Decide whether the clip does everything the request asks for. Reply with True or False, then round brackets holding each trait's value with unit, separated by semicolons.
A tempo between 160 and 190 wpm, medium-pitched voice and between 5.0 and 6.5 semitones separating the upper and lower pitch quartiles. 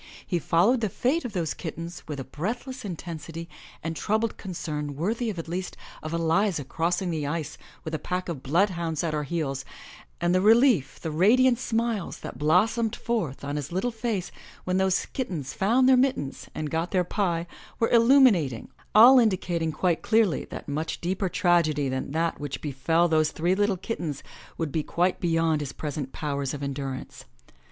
True (175 wpm; 170 Hz; 5.4 semitones)